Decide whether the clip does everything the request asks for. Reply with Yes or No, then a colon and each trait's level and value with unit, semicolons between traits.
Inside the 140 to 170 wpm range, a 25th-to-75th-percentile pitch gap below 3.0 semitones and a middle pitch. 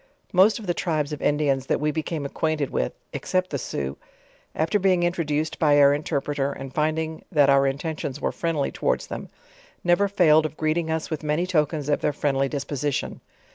No: average, 185 wpm; narrow, 2.5 semitones; medium, 150 Hz